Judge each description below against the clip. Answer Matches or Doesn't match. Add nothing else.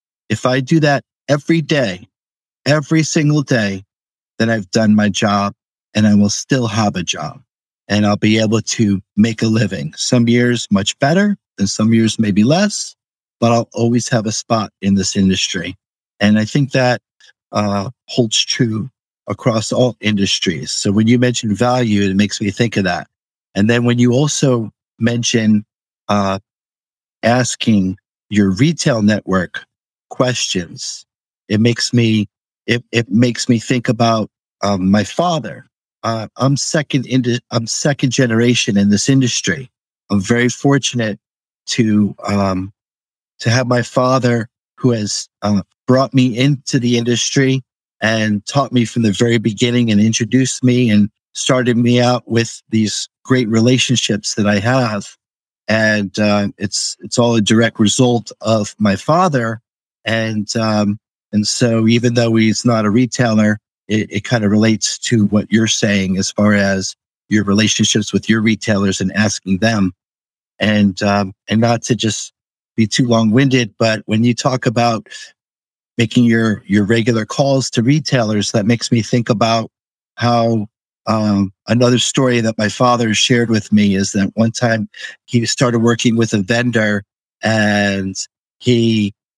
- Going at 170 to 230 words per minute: Doesn't match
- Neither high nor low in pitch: Doesn't match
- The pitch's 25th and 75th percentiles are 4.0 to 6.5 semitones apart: Doesn't match